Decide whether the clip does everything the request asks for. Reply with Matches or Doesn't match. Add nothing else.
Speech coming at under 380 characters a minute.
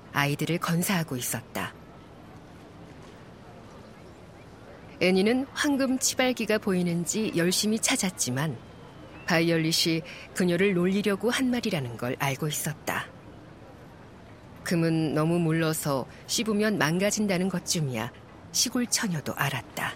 Matches